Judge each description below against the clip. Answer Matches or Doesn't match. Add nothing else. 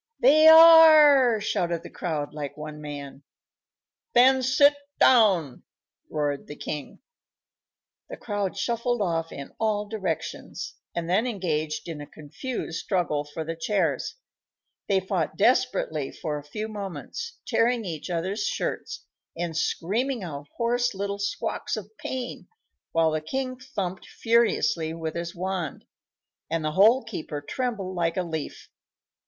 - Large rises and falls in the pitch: Matches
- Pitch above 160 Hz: Matches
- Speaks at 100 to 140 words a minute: Matches